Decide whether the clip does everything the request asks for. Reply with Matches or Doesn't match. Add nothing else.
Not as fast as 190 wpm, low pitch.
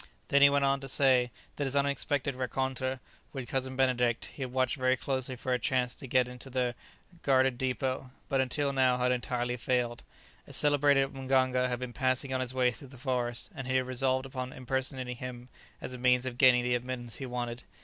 Doesn't match